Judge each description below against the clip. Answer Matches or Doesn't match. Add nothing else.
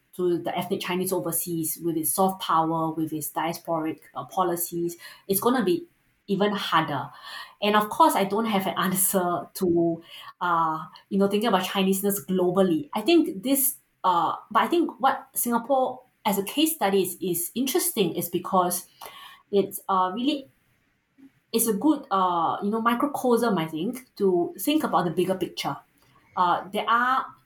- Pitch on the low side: Doesn't match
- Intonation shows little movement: Doesn't match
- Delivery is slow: Doesn't match